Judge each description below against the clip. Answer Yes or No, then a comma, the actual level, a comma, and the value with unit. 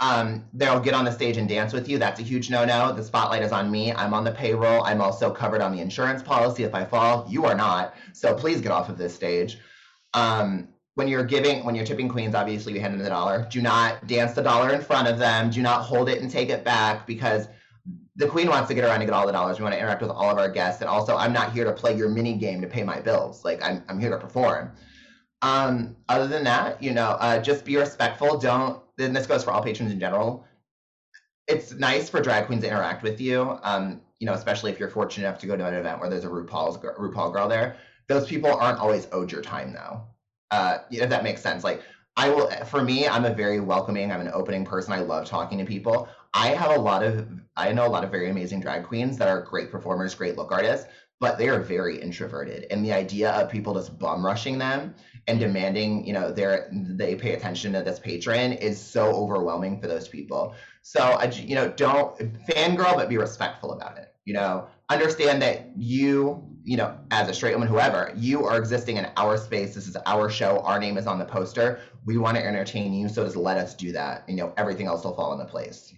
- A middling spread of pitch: Yes, average, 3.7 semitones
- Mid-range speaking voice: No, low, 115 Hz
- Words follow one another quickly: Yes, fast, 240 wpm